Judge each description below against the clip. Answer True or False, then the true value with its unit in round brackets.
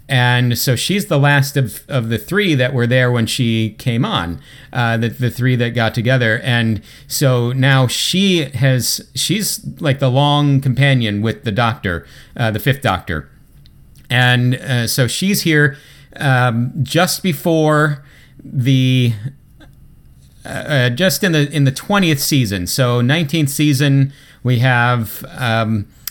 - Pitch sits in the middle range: False (130 Hz)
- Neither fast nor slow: True (145 wpm)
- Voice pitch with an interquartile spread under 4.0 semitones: True (3.1 semitones)